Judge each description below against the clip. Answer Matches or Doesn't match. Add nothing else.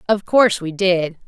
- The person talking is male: Doesn't match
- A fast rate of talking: Doesn't match